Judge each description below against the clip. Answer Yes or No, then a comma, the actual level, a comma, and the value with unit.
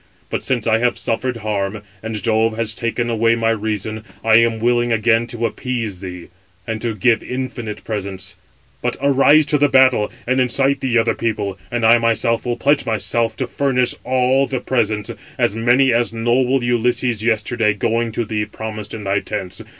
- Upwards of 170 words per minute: Yes, average, 180 wpm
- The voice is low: Yes, low, 115 Hz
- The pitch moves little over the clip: Yes, narrow, 2.2 semitones